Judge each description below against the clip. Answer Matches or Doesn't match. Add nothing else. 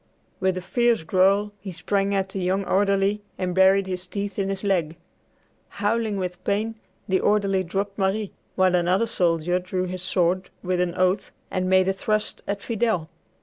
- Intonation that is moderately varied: Doesn't match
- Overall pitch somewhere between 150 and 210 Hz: Matches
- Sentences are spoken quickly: Doesn't match